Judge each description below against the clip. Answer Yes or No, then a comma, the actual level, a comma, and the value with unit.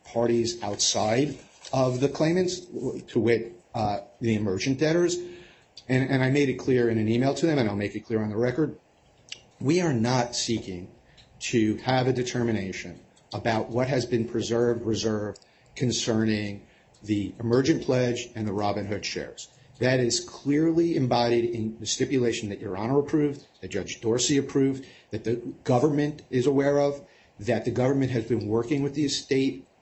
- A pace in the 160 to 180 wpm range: Yes, average, 165 wpm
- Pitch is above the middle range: No, low, 120 Hz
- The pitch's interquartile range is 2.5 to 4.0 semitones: Yes, average, 3.4 semitones